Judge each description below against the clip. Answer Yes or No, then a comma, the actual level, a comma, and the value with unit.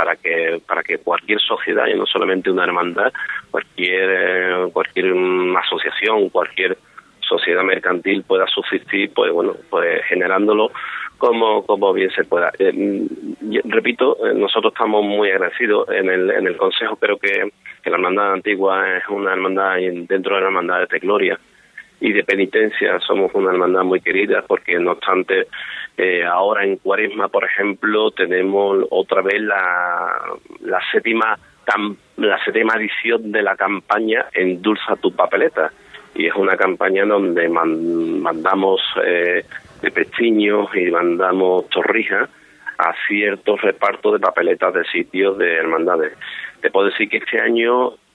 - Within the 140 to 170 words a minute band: Yes, average, 145 wpm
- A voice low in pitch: Yes, low, 110 Hz